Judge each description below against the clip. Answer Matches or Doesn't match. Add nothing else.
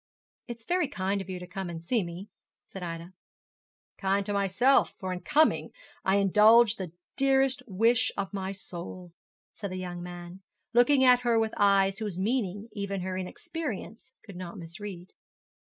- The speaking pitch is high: Matches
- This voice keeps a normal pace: Matches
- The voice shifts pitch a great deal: Doesn't match